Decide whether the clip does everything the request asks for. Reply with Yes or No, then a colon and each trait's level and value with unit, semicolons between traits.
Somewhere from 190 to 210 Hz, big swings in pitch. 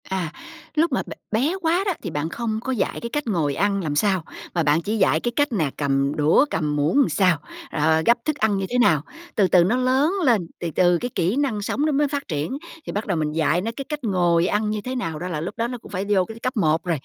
Yes: high, 200 Hz; wide, 7.2 semitones